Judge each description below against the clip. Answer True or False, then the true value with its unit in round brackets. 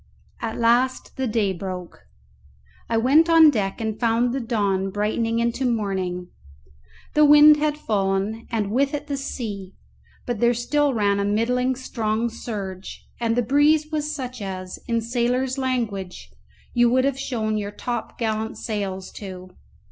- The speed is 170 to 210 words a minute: False (155 wpm)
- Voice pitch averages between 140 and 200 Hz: False (230 Hz)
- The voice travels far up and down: False (4.2 semitones)